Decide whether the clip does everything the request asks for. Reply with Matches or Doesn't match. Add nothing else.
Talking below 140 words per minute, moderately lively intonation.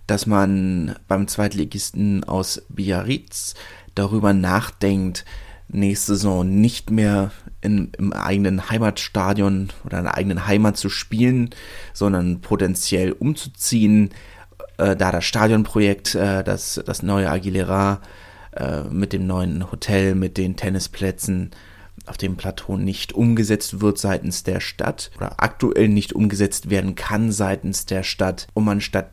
Doesn't match